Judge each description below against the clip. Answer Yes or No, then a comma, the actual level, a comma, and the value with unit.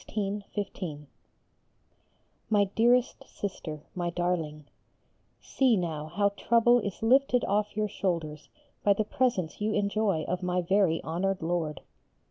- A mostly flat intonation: No, average, 3.9 semitones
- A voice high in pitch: Yes, high, 195 Hz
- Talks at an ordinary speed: No, slow, 120 wpm